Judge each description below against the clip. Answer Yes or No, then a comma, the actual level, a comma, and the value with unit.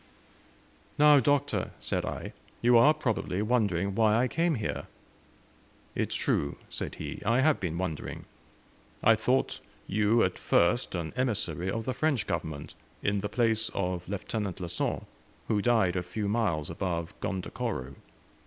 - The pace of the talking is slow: No, average, 150 wpm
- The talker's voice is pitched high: No, low, 105 Hz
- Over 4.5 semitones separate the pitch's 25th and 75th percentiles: Yes, average, 5.2 semitones